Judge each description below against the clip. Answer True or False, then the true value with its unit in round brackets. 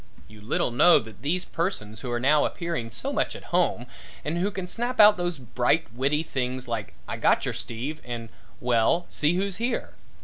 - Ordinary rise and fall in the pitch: False (6.8 semitones)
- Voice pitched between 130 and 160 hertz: True (140 Hz)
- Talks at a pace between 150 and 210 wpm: True (190 wpm)